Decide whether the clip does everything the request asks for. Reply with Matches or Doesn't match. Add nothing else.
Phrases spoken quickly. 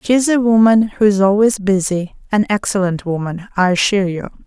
Doesn't match